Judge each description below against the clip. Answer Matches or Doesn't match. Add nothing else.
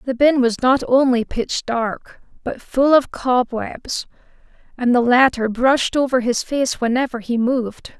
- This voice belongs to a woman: Matches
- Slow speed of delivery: Doesn't match